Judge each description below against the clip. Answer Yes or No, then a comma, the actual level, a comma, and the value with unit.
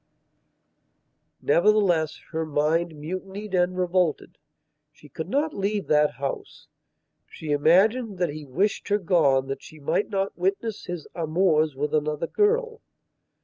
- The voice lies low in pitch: No, medium, 175 Hz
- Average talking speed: No, slow, 130 wpm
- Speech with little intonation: No, average, 4.6 semitones